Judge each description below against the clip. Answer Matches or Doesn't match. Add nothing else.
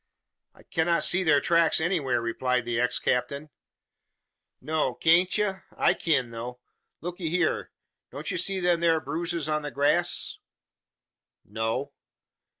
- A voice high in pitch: Doesn't match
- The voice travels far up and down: Doesn't match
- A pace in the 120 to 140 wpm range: Matches